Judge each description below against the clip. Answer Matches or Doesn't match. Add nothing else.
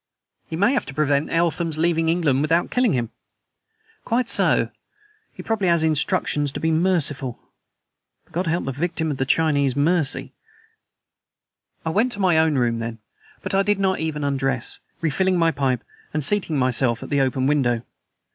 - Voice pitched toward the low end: Doesn't match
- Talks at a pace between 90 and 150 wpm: Doesn't match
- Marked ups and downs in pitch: Doesn't match